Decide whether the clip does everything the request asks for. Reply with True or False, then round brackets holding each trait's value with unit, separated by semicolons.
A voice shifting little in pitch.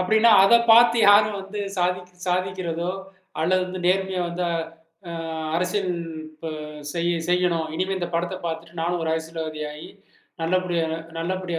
True (2.0 semitones)